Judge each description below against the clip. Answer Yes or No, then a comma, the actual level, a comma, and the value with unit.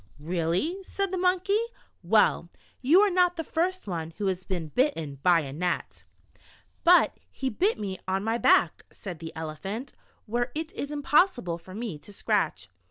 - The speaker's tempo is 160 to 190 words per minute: Yes, average, 170 wpm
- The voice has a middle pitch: No, high, 215 Hz